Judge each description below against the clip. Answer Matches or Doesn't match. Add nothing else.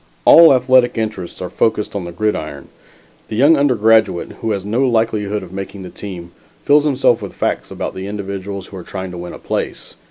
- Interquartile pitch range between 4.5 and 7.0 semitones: Doesn't match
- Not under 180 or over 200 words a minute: Matches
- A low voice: Matches